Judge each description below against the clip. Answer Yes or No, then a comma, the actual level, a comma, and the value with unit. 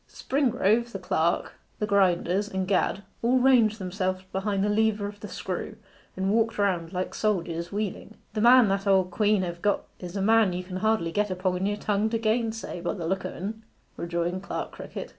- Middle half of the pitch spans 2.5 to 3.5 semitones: Yes, average, 2.9 semitones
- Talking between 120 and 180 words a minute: No, average, 200 wpm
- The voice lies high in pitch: Yes, high, 200 Hz